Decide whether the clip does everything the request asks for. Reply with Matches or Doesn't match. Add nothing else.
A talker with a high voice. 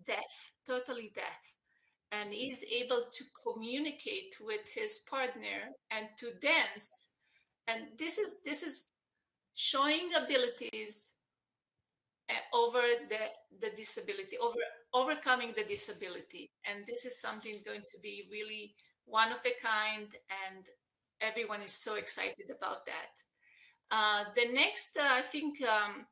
Matches